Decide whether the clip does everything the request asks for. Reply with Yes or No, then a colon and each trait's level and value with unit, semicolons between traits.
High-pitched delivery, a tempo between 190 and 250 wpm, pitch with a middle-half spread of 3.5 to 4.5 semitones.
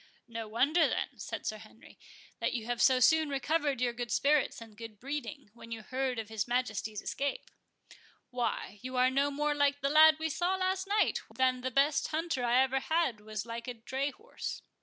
Yes: very high, 260 Hz; average, 200 wpm; average, 4.2 semitones